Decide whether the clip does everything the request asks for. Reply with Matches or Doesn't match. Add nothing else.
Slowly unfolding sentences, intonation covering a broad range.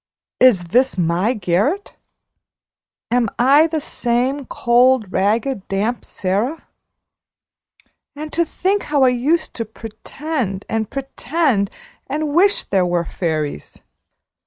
Matches